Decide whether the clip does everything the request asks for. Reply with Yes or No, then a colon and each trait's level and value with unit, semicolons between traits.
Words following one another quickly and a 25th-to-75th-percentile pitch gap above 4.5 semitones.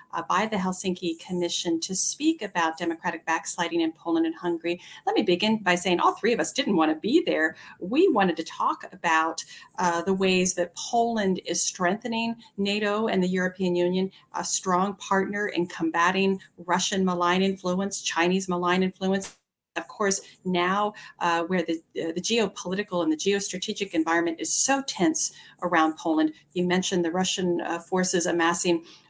No: fast, 165 wpm; narrow, 2.4 semitones